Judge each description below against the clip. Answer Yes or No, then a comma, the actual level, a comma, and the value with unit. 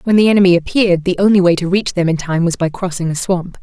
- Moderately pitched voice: Yes, medium, 180 Hz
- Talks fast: Yes, fast, 280 wpm